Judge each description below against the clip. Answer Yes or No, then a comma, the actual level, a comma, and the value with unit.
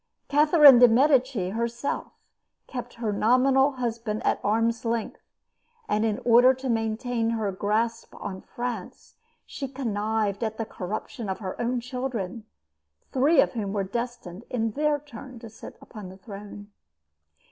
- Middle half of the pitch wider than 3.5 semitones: No, average, 3.1 semitones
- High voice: Yes, high, 230 Hz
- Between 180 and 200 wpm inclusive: No, average, 145 wpm